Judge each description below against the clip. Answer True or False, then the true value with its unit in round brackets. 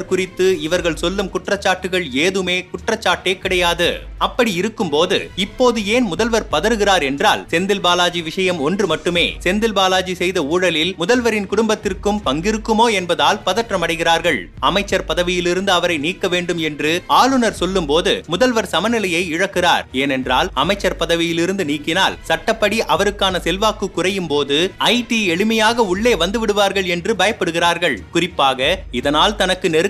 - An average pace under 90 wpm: False (125 wpm)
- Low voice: False (185 Hz)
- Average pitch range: True (3.4 semitones)